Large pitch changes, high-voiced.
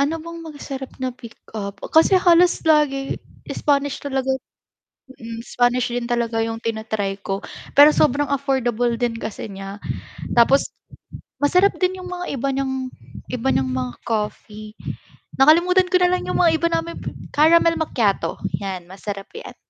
Yes: wide, 6.1 semitones; very high, 265 Hz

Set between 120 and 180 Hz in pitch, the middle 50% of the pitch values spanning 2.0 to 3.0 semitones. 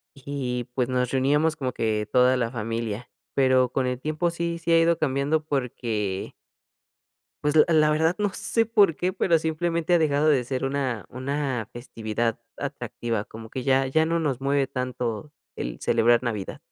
No: low, 135 Hz; average, 4.5 semitones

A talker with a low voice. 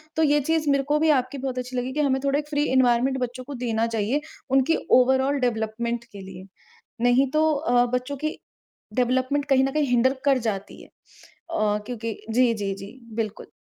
No: very high, 255 Hz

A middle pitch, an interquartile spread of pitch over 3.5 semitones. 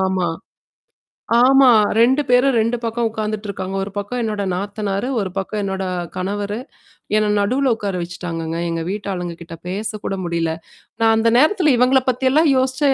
No: high, 210 Hz; average, 4.6 semitones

